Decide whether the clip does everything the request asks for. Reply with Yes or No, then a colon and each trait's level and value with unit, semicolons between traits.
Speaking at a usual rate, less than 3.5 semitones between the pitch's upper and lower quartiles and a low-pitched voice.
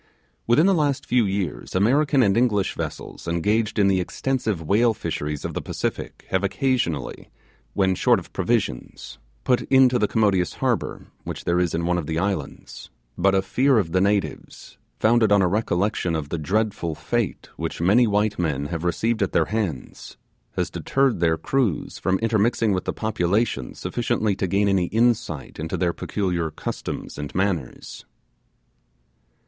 No: average, 165 wpm; average, 4.8 semitones; low, 100 Hz